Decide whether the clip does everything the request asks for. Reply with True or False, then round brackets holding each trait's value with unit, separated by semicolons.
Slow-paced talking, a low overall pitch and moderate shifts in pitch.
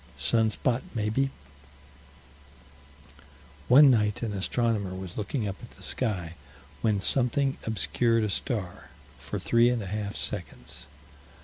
True (125 wpm; 110 Hz; 3.3 semitones)